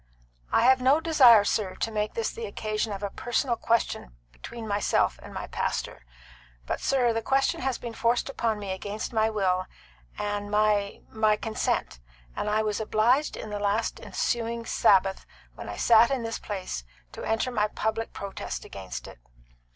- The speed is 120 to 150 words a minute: No, average, 175 wpm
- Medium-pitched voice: No, high, 220 Hz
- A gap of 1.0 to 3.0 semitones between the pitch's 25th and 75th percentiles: Yes, narrow, 2.5 semitones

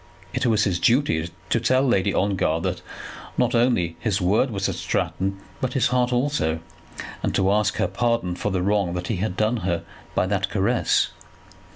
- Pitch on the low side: Yes, low, 105 Hz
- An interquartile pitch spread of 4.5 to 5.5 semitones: Yes, average, 4.9 semitones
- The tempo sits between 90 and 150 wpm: No, average, 185 wpm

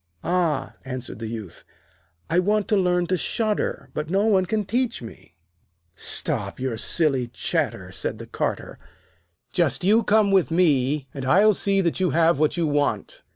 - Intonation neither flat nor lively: No, wide, 6.1 semitones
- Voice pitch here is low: No, medium, 170 Hz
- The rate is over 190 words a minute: No, average, 165 wpm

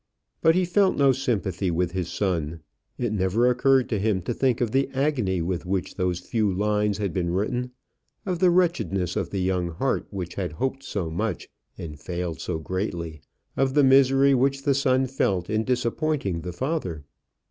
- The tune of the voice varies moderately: No, wide, 6.8 semitones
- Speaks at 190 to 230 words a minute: No, average, 180 wpm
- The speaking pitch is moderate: No, low, 105 Hz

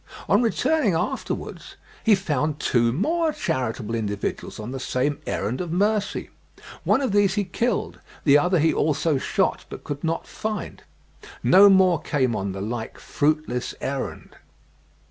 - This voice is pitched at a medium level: Yes, medium, 155 Hz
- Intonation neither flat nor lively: No, wide, 8.0 semitones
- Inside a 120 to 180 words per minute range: Yes, average, 145 wpm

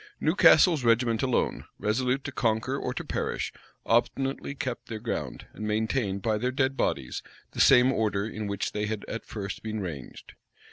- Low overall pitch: Yes, low, 115 Hz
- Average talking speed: Yes, average, 170 wpm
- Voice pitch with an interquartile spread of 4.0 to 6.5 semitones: No, average, 3.3 semitones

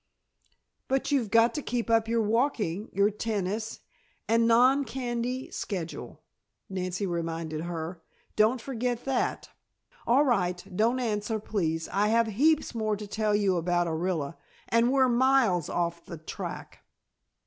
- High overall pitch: Yes, high, 215 Hz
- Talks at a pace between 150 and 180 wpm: No, slow, 135 wpm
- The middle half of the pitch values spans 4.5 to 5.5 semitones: Yes, average, 5.0 semitones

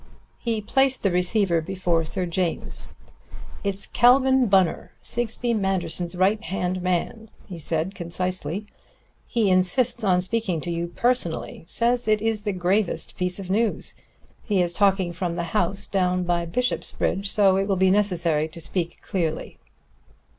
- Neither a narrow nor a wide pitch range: Yes, average, 3.3 semitones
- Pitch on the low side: No, high, 190 Hz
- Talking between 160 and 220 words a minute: No, average, 145 wpm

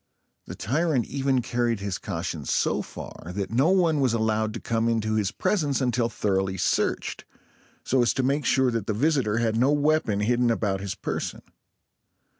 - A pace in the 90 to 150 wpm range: No, average, 175 wpm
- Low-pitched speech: Yes, low, 115 Hz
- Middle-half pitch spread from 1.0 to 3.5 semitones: No, average, 3.9 semitones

